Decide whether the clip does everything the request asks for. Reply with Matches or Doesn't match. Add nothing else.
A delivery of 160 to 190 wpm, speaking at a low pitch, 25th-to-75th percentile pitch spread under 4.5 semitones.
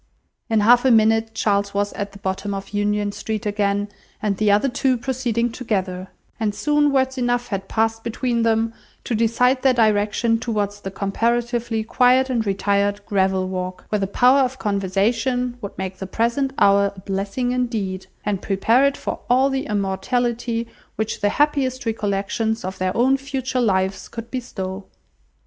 Doesn't match